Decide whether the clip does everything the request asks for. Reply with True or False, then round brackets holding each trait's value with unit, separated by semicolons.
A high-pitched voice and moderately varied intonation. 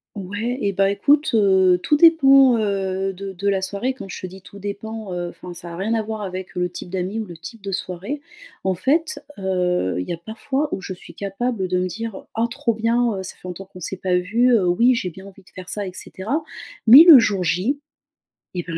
True (195 Hz; 3.9 semitones)